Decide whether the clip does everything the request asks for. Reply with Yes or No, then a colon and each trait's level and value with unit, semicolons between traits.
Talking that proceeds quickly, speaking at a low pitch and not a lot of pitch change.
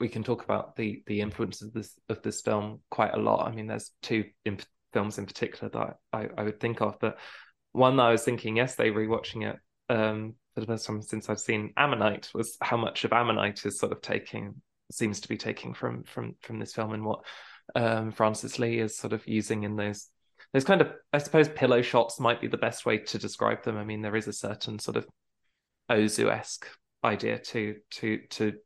Yes: fast, 220 wpm; low, 110 Hz; narrow, 1.7 semitones